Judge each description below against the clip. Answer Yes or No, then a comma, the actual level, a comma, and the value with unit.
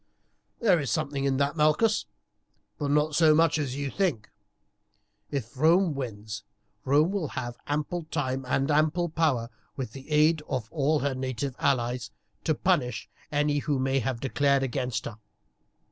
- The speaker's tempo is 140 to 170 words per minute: Yes, average, 155 wpm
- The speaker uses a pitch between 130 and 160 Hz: Yes, medium, 140 Hz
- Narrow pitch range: No, average, 3.1 semitones